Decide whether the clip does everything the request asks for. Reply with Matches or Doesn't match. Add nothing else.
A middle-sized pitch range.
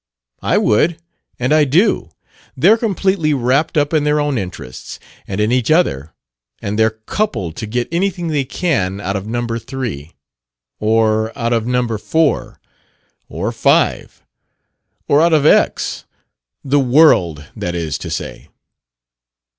Doesn't match